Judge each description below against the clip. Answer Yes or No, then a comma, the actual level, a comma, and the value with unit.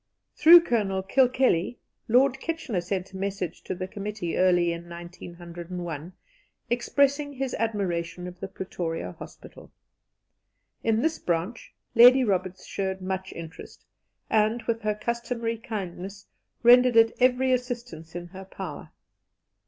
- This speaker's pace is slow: Yes, slow, 125 wpm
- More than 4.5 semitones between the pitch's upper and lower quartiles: Yes, average, 5.3 semitones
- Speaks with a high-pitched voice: Yes, high, 200 Hz